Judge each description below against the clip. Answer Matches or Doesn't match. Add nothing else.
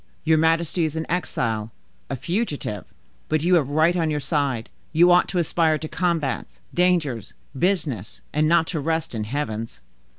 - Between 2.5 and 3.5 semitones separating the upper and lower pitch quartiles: Doesn't match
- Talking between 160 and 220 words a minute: Matches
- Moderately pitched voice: Matches